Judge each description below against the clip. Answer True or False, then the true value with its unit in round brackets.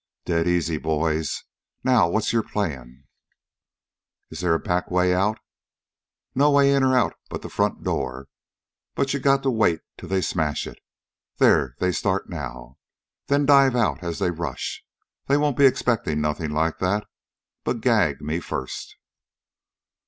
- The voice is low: True (90 Hz)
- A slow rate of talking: False (150 wpm)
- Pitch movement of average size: False (8.1 semitones)